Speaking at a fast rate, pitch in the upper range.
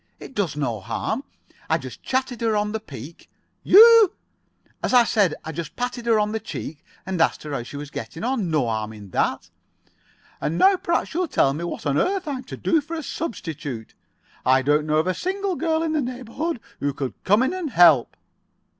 Yes: fast, 210 wpm; high, 210 Hz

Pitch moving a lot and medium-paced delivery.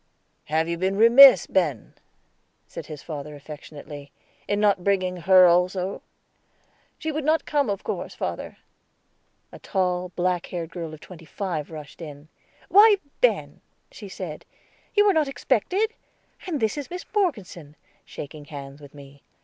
Yes: wide, 7.5 semitones; average, 150 wpm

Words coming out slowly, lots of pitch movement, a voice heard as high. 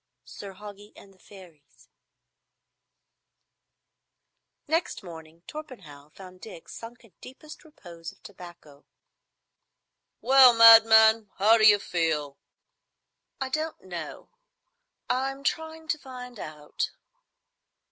Yes: slow, 95 wpm; wide, 7.0 semitones; high, 210 Hz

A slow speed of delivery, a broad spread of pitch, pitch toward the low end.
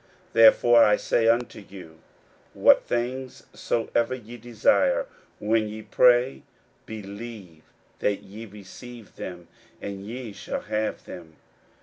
No: slow, 120 wpm; average, 3.2 semitones; low, 110 Hz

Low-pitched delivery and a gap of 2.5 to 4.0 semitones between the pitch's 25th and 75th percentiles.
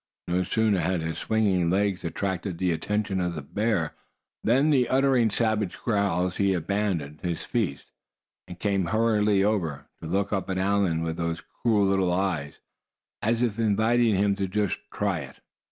Yes: very low, 95 Hz; average, 3.4 semitones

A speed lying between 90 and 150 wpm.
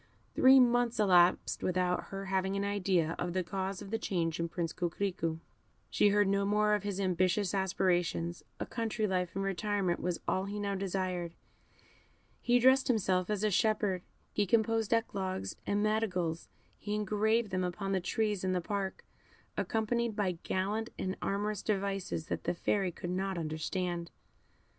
No: average, 160 wpm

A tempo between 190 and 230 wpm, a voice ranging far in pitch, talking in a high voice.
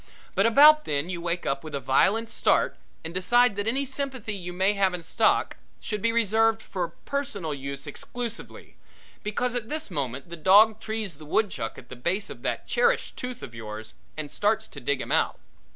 Yes: average, 195 wpm; wide, 6.7 semitones; high, 200 Hz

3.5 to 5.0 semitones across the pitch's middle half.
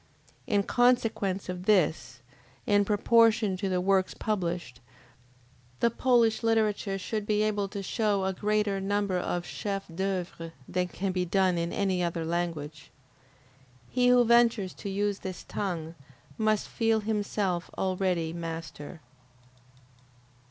No: average, 3.1 semitones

